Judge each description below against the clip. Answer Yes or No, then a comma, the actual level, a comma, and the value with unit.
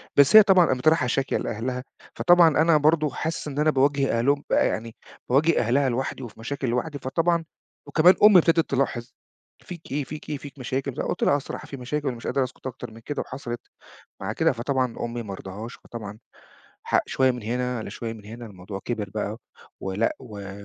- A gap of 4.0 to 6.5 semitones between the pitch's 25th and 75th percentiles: Yes, average, 4.3 semitones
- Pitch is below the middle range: Yes, low, 130 Hz